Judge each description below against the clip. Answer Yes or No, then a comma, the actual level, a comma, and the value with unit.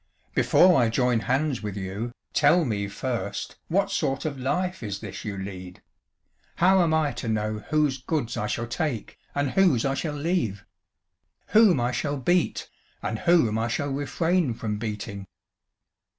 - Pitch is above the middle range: No, low, 130 Hz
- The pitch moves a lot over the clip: Yes, wide, 6.6 semitones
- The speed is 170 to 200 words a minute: No, average, 160 wpm